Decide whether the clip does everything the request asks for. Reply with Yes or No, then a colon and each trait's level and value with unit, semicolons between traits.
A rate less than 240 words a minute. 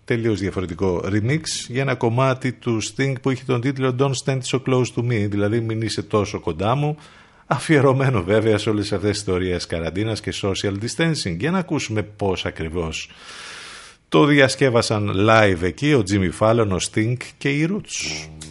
Yes: fast, 170 wpm